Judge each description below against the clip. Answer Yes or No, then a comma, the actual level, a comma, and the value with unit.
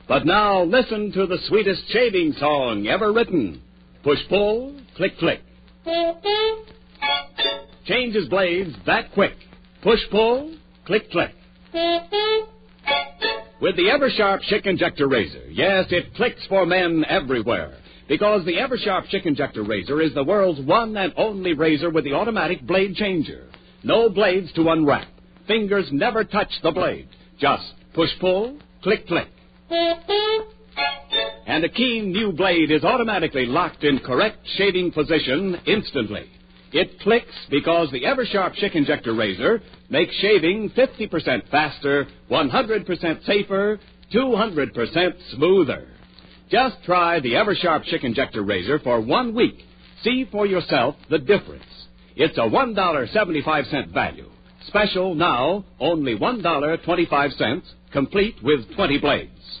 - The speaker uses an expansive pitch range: Yes, wide, 6.7 semitones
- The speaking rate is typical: No, slow, 125 wpm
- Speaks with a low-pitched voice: No, medium, 185 Hz